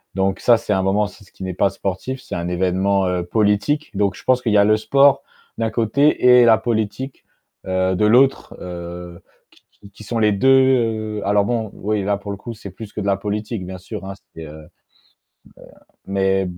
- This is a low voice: Yes, low, 105 Hz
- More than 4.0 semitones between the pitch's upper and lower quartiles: No, average, 3.0 semitones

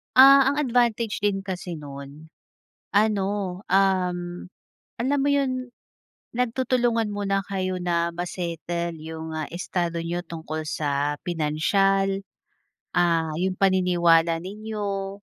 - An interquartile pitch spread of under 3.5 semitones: No, average, 4.0 semitones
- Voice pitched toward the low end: No, medium, 185 Hz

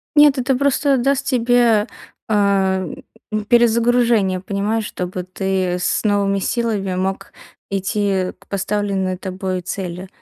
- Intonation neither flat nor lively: Yes, average, 3.8 semitones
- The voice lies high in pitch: Yes, high, 200 Hz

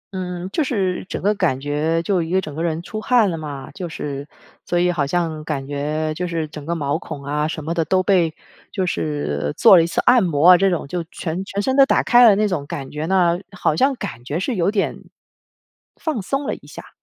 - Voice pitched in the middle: Yes, medium, 170 Hz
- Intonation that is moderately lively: Yes, average, 4.2 semitones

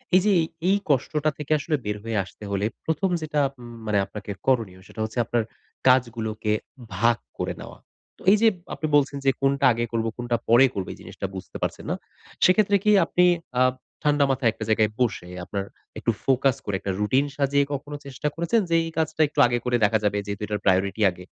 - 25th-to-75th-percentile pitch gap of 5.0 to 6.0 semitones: Yes, wide, 5.6 semitones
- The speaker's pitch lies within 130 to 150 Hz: No, low, 120 Hz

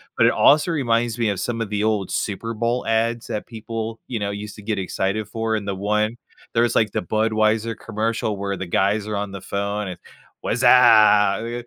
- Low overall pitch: Yes, low, 110 Hz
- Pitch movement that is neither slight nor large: No, narrow, 2.1 semitones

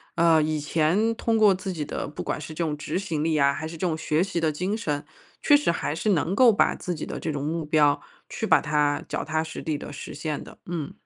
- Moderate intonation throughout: Yes, average, 3.2 semitones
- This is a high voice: No, medium, 160 Hz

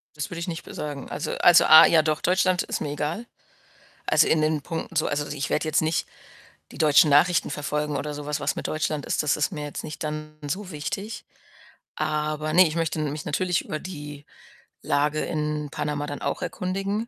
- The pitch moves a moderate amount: No, narrow, 2.0 semitones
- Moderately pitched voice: Yes, medium, 155 Hz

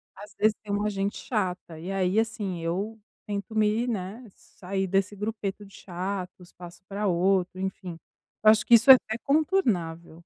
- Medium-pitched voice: No, high, 200 Hz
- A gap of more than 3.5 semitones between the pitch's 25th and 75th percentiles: No, average, 2.8 semitones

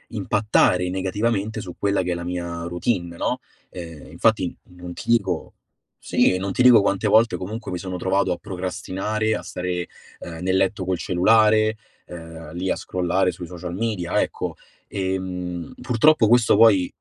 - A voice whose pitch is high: No, very low, 95 Hz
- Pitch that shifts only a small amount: No, average, 3.3 semitones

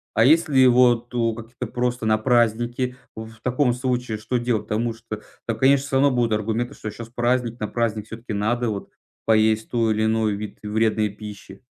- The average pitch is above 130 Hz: No, low, 115 Hz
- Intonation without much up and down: Yes, narrow, 2.2 semitones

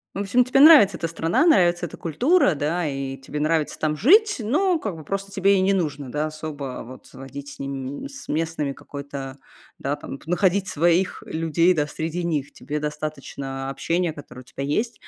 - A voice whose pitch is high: No, medium, 160 Hz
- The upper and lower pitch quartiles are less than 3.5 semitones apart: No, average, 5.3 semitones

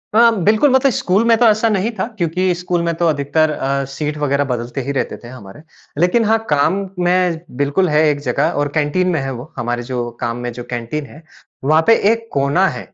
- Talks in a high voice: No, medium, 150 Hz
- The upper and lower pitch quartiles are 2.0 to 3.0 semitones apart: No, average, 5.2 semitones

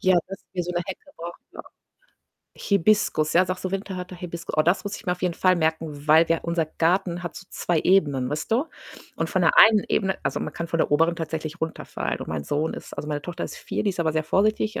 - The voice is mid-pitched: Yes, medium, 170 Hz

